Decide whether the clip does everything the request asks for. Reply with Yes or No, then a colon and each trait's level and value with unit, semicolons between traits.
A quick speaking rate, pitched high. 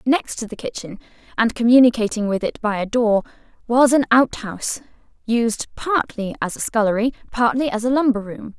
No: average, 170 wpm; high, 235 Hz